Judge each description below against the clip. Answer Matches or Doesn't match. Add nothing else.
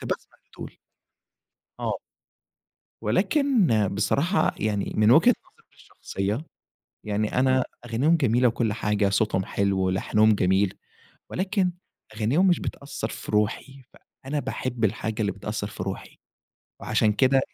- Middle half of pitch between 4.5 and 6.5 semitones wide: Matches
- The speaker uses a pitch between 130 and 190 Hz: Doesn't match